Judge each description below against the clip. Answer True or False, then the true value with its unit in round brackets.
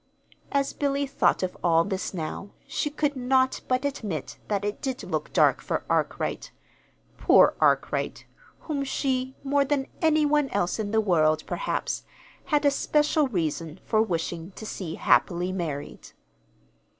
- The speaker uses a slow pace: False (150 wpm)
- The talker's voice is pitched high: True (225 Hz)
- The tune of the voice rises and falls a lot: True (8.0 semitones)